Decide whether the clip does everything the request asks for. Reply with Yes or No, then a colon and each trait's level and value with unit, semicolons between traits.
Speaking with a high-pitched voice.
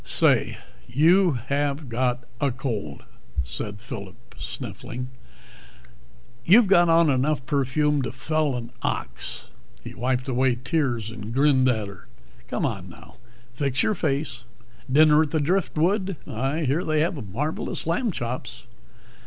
No: low, 135 Hz